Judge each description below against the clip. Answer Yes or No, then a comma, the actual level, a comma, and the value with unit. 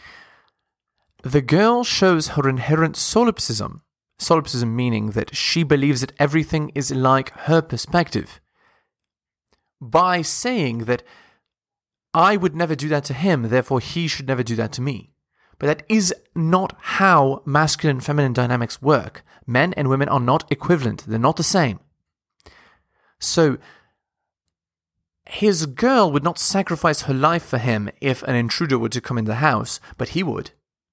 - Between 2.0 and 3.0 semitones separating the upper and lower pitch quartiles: No, average, 5.1 semitones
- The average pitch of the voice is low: No, medium, 145 Hz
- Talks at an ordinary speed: Yes, average, 150 wpm